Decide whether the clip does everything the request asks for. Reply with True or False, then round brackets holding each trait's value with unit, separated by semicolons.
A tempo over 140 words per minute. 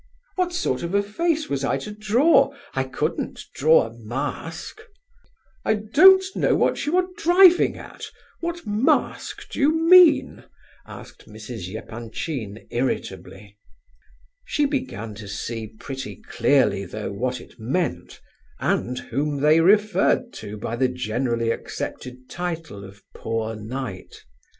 False (135 wpm)